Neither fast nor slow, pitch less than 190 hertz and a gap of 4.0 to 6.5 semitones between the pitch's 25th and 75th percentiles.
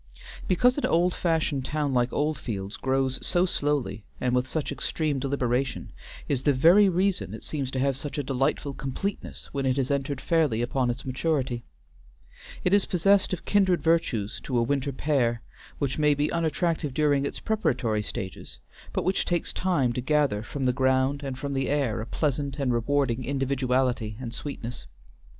No: average, 170 wpm; medium, 140 Hz; average, 3.4 semitones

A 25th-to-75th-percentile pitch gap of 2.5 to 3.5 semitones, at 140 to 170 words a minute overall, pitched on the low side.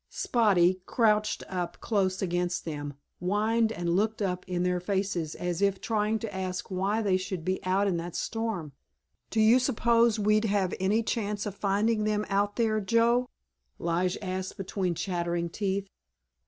No: average, 3.0 semitones; average, 160 wpm; high, 195 Hz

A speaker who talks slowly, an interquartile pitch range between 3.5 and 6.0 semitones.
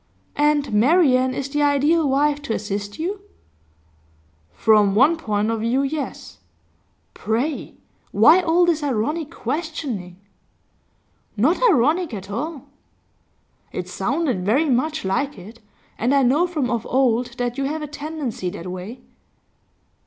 Yes: slow, 130 wpm; wide, 5.6 semitones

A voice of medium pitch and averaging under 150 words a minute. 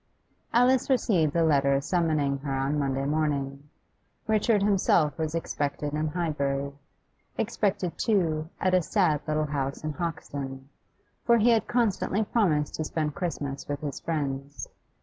Yes: medium, 155 Hz; average, 140 wpm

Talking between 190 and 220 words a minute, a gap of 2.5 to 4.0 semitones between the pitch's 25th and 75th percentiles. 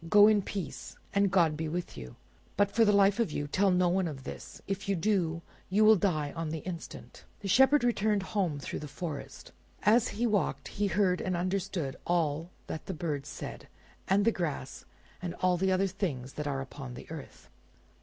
No: average, 200 wpm; average, 4.6 semitones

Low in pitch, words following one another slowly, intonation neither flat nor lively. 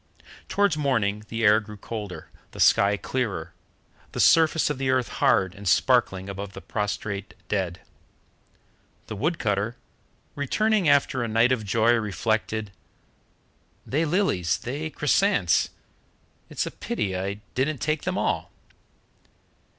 No: low, 110 Hz; slow, 130 wpm; wide, 6.0 semitones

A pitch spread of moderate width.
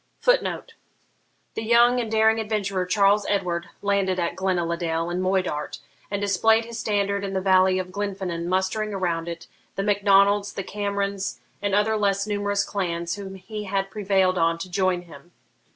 No: narrow, 2.0 semitones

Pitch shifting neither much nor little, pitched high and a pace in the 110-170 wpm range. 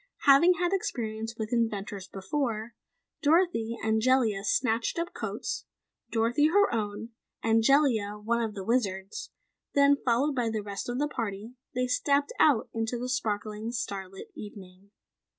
Yes: average, 3.9 semitones; high, 230 Hz; average, 145 wpm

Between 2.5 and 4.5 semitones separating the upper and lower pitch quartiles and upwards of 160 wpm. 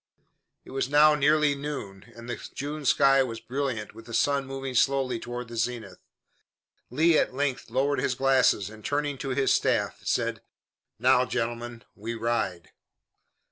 No: average, 3.1 semitones; average, 155 wpm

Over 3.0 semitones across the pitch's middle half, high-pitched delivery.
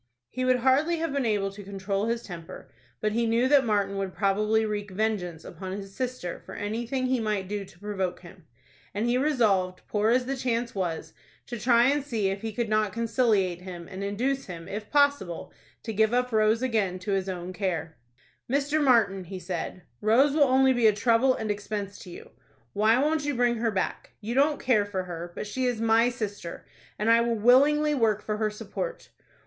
Yes: average, 4.2 semitones; high, 215 Hz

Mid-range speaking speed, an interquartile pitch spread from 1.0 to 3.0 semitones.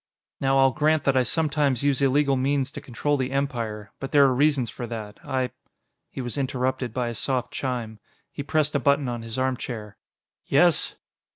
Yes: average, 190 wpm; narrow, 2.6 semitones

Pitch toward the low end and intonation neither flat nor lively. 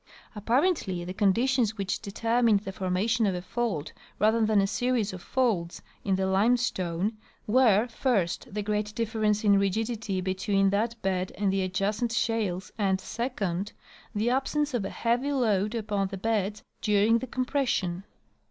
No: high, 210 Hz; average, 3.3 semitones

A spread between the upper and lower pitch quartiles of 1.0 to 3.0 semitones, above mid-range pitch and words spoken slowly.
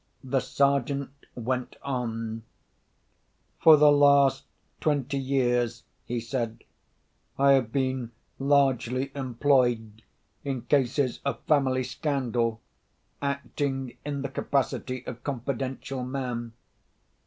No: narrow, 2.4 semitones; low, 130 Hz; slow, 95 wpm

